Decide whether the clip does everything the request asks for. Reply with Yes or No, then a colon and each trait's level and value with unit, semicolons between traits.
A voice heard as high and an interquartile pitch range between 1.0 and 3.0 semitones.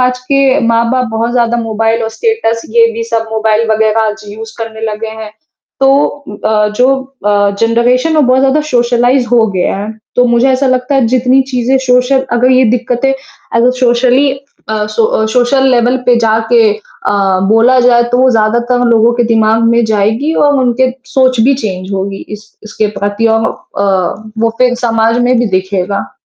Yes: high, 235 Hz; narrow, 2.4 semitones